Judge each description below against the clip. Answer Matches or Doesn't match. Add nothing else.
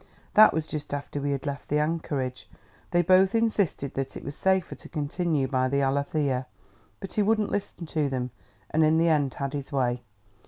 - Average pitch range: Matches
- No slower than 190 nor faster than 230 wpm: Matches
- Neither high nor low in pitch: Matches